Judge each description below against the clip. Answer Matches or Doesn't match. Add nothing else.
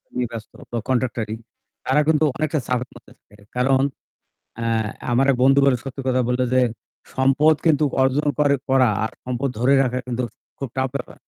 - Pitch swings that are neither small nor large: Doesn't match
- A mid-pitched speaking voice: Doesn't match